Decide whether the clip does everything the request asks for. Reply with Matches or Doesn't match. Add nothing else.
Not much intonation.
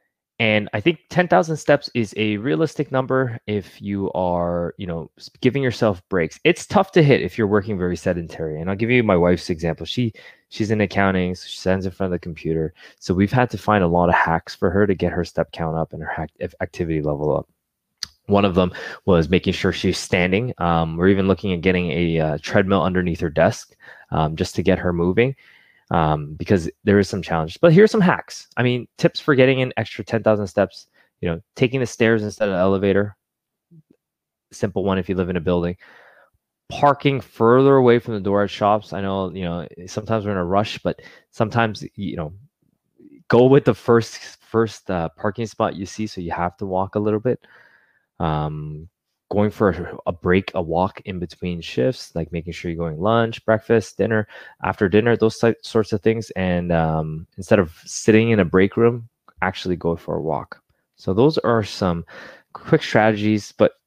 Doesn't match